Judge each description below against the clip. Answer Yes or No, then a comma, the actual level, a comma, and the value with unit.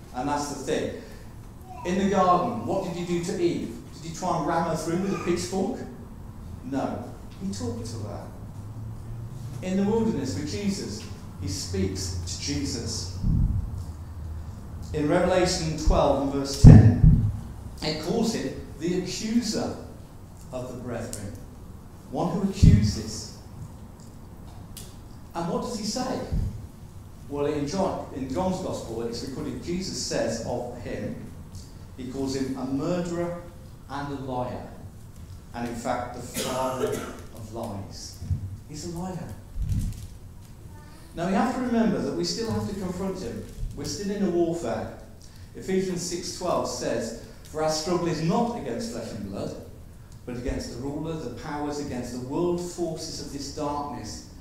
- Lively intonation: Yes, wide, 8.4 semitones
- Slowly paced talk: No, average, 145 wpm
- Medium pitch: No, low, 125 Hz